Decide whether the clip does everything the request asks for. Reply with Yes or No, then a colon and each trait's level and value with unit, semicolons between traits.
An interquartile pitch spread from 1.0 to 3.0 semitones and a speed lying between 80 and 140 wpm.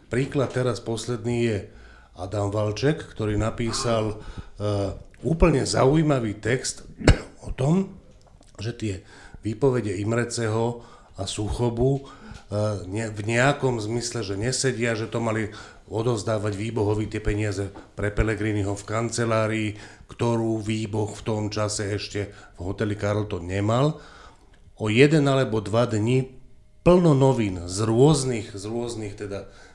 Yes: narrow, 2.6 semitones; average, 120 wpm